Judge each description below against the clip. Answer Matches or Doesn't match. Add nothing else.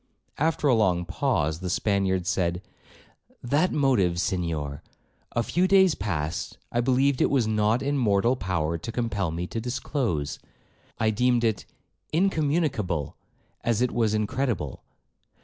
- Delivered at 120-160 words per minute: Matches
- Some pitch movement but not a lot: Doesn't match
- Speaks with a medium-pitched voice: Doesn't match